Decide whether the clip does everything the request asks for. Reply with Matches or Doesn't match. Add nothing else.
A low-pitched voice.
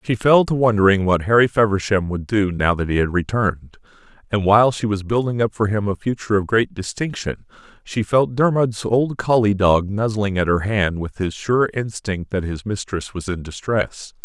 Matches